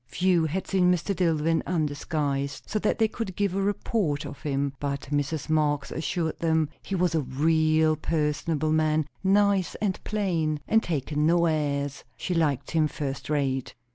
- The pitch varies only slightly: No, average, 3.5 semitones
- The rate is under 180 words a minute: Yes, average, 165 wpm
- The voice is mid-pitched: Yes, medium, 155 Hz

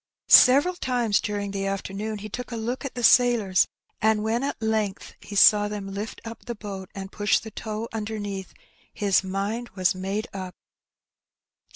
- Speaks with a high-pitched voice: Yes, high, 210 Hz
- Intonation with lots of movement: No, narrow, 2.6 semitones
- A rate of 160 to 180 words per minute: Yes, average, 175 wpm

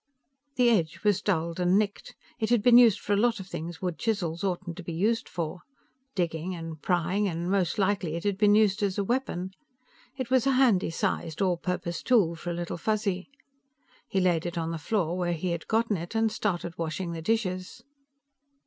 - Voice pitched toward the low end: No, medium, 185 Hz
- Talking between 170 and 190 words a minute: No, average, 200 wpm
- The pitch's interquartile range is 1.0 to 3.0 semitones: No, average, 3.9 semitones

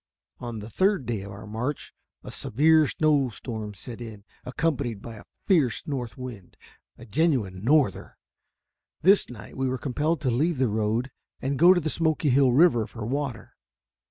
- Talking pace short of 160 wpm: No, average, 170 wpm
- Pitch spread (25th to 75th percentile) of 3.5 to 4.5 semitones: No, average, 5.2 semitones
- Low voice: Yes, low, 125 Hz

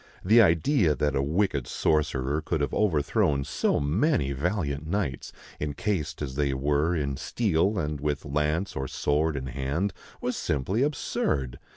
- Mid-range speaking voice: No, very low, 75 Hz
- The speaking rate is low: No, average, 150 wpm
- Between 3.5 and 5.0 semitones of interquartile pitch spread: Yes, average, 4.3 semitones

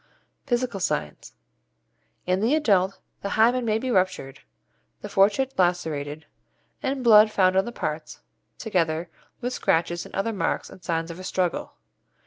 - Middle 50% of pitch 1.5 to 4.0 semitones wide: No, average, 5.1 semitones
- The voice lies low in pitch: No, high, 190 Hz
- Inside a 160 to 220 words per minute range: No, average, 145 wpm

